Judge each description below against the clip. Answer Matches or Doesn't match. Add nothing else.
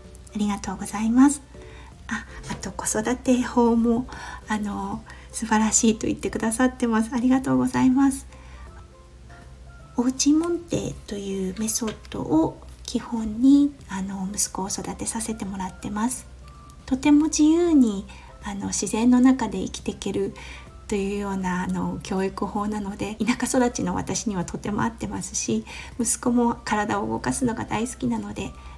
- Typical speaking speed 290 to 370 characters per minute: Matches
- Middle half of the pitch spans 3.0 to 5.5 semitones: Matches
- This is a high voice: Matches